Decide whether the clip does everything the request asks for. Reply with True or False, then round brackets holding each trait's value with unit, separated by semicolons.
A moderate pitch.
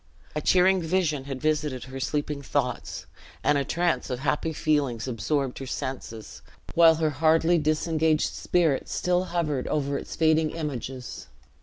True (150 Hz)